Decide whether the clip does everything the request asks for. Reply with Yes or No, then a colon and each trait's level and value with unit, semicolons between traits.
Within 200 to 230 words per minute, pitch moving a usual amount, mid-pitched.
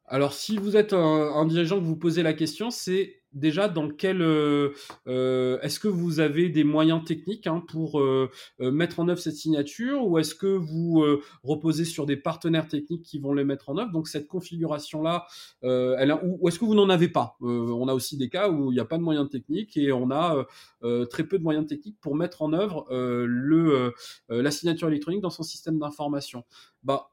Yes: fast, 220 wpm; average, 3.3 semitones; medium, 155 Hz